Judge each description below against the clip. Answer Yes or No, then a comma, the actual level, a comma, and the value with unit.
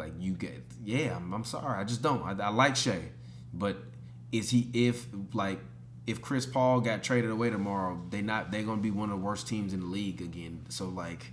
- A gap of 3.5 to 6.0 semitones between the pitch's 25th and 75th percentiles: Yes, wide, 5.6 semitones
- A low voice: Yes, low, 100 Hz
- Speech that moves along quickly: Yes, fast, 220 wpm